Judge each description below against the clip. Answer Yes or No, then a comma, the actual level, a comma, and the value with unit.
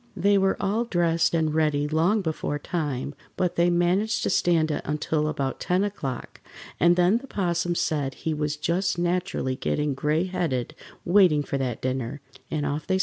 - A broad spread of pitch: No, average, 3.5 semitones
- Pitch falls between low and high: Yes, medium, 165 Hz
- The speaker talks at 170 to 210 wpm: Yes, average, 180 wpm